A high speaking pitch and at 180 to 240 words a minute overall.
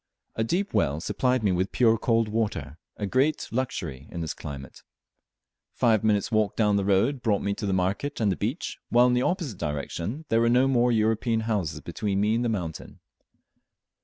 No: low, 110 Hz; average, 190 wpm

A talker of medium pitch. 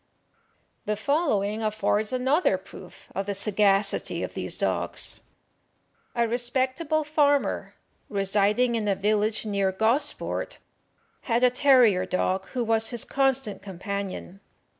No: high, 220 Hz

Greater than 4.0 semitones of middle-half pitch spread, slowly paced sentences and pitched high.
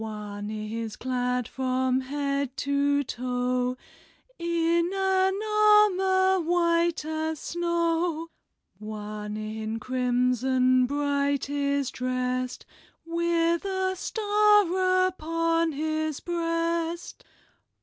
Yes: average, 5.3 semitones; slow, 95 wpm; very high, 290 Hz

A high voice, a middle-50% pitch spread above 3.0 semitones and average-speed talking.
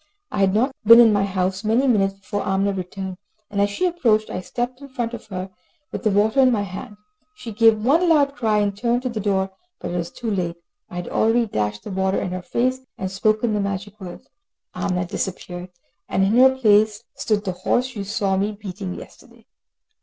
No: high, 205 Hz; average, 3.6 semitones; fast, 215 wpm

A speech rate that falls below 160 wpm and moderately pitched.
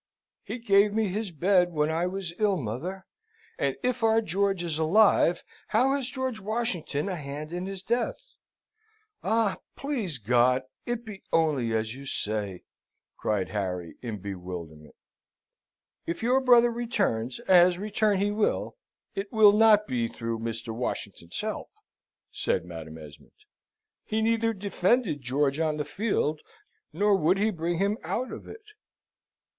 Yes: average, 145 wpm; medium, 180 Hz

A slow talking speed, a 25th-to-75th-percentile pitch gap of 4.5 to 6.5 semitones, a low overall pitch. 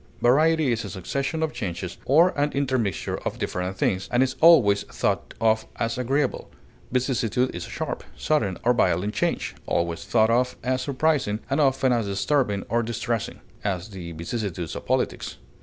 No: average, 160 wpm; average, 5.2 semitones; low, 120 Hz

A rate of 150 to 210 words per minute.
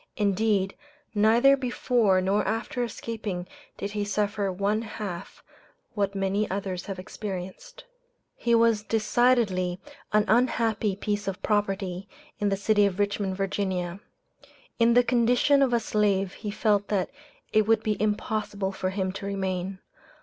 No: average, 140 wpm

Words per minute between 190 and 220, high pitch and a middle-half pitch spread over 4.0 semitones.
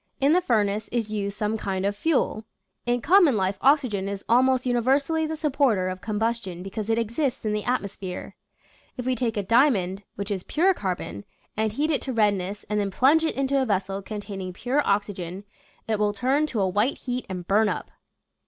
Yes: average, 200 wpm; high, 215 Hz; average, 4.7 semitones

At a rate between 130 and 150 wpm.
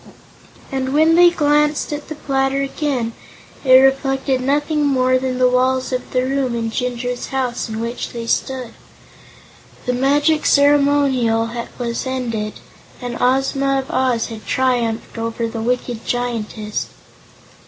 Yes: slow, 135 wpm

